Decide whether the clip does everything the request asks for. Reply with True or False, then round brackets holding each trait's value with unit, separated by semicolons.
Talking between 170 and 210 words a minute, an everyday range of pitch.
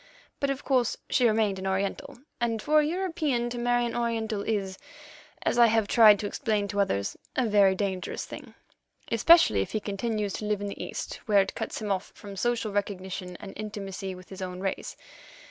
True (195 wpm; 3.5 semitones)